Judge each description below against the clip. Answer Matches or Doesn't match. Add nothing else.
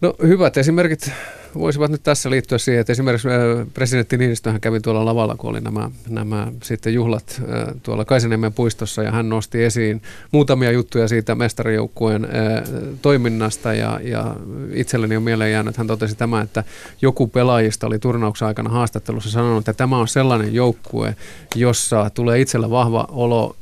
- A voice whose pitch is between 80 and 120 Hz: Matches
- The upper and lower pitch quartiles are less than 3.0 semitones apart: Matches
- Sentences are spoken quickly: Matches